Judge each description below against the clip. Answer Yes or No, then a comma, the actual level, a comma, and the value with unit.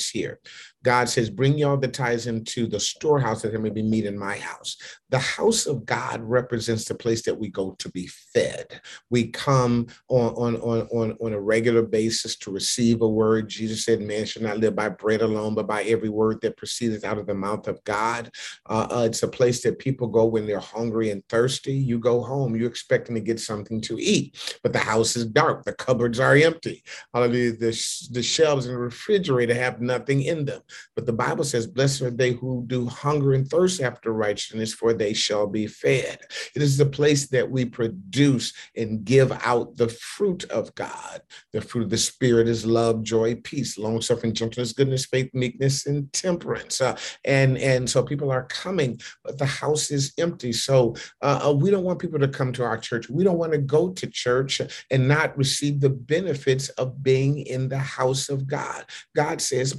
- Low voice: Yes, low, 120 Hz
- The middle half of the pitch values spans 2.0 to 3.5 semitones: Yes, average, 3.2 semitones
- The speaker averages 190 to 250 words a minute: Yes, fast, 205 wpm